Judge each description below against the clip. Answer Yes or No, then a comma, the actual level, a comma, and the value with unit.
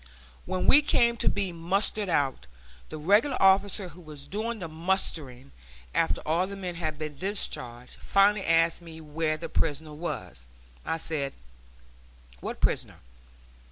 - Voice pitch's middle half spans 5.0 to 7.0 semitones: No, average, 4.2 semitones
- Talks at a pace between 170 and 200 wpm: No, average, 145 wpm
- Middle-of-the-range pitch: Yes, medium, 165 Hz